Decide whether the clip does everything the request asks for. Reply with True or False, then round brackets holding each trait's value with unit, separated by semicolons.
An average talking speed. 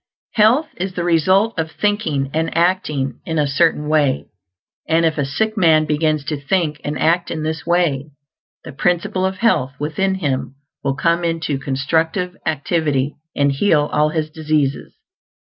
True (160 wpm)